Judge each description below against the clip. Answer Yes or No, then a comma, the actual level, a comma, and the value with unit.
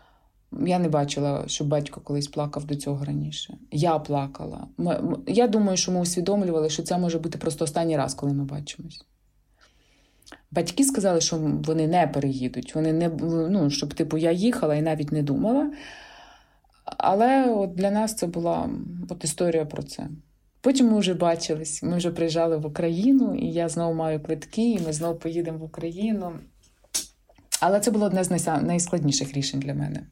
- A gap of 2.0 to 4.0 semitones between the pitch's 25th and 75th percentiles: Yes, average, 3.4 semitones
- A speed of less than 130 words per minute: No, fast, 165 wpm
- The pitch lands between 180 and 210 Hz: No, medium, 165 Hz